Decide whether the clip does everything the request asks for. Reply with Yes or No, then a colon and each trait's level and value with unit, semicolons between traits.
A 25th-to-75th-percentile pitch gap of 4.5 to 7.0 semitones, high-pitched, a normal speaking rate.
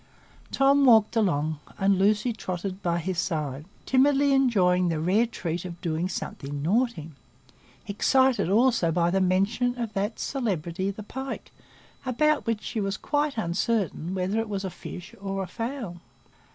Yes: average, 5.3 semitones; high, 195 Hz; average, 150 wpm